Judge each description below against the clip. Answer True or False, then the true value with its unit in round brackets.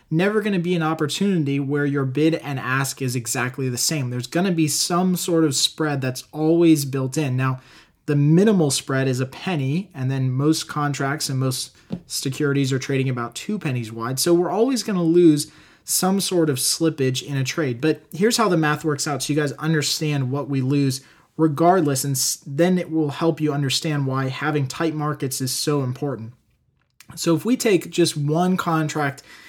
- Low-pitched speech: False (150 Hz)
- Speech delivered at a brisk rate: False (195 wpm)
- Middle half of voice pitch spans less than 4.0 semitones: True (3.6 semitones)